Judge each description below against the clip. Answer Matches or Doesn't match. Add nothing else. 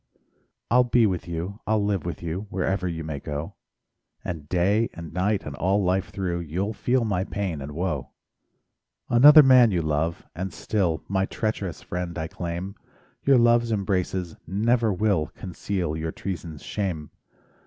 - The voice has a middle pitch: Doesn't match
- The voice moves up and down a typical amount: Matches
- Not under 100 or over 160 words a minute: Matches